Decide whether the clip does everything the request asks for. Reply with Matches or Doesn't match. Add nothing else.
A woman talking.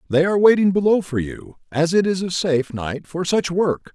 Doesn't match